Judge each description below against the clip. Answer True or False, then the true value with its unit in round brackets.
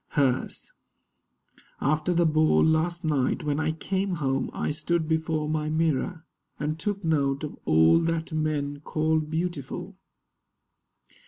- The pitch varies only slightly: True (1.8 semitones)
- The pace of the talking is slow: True (130 wpm)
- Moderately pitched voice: True (155 Hz)